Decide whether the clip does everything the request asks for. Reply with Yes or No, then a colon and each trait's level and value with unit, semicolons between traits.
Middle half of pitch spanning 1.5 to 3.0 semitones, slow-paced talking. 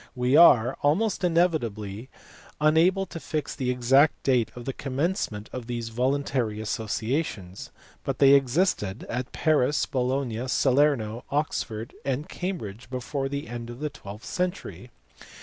No: average, 4.3 semitones; slow, 130 wpm